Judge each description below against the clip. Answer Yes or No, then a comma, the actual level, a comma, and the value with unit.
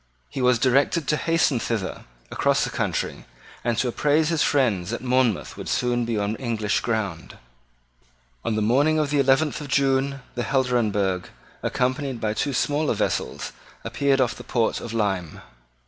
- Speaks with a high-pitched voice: No, low, 125 Hz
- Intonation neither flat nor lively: Yes, average, 3.9 semitones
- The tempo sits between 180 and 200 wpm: No, average, 165 wpm